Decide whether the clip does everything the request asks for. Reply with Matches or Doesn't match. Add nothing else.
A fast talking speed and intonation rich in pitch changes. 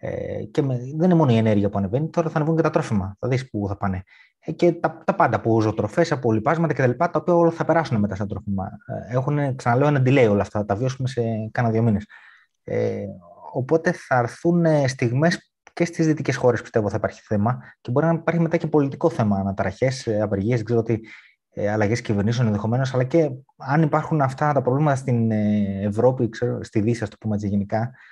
Matches